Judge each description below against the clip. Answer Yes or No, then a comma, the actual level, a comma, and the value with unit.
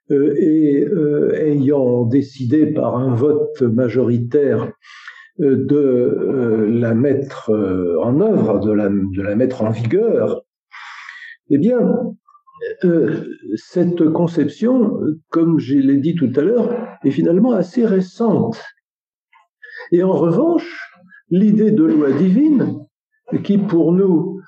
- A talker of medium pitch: Yes, medium, 165 Hz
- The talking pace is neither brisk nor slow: No, slow, 120 wpm